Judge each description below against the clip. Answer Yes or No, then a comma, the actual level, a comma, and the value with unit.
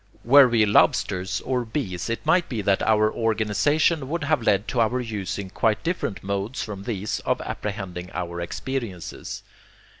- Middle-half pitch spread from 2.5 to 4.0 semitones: No, average, 4.5 semitones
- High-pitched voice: No, low, 110 Hz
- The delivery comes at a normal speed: Yes, average, 155 wpm